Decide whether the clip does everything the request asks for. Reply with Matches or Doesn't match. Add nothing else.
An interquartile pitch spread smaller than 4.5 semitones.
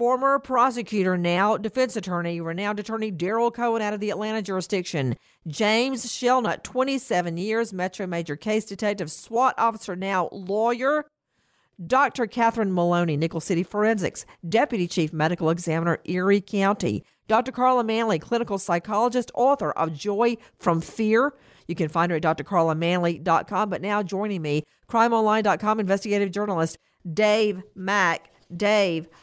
Doesn't match